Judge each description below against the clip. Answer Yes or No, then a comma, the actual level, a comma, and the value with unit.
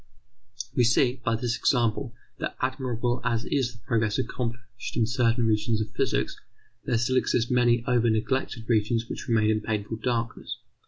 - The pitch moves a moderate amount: No, narrow, 1.6 semitones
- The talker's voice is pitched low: Yes, low, 115 Hz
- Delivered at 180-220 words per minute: No, average, 160 wpm